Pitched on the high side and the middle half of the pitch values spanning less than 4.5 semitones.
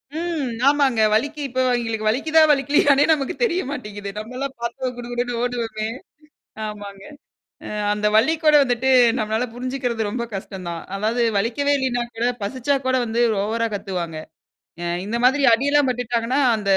Yes: high, 245 Hz; average, 4.0 semitones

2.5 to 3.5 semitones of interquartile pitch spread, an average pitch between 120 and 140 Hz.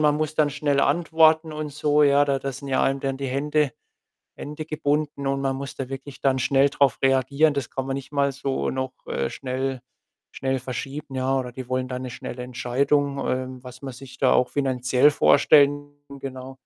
No: narrow, 1.8 semitones; low, 135 Hz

